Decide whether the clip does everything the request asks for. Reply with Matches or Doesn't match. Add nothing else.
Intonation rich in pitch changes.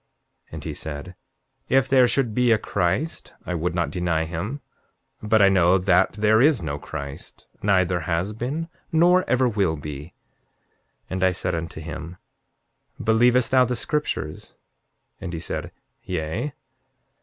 Matches